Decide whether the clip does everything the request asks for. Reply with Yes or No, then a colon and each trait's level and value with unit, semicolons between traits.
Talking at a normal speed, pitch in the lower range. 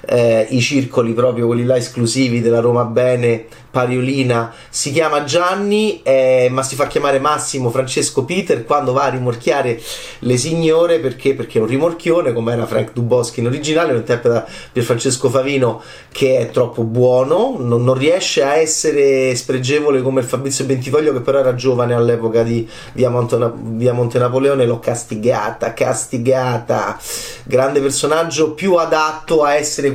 Yes: average, 155 wpm; low, 130 Hz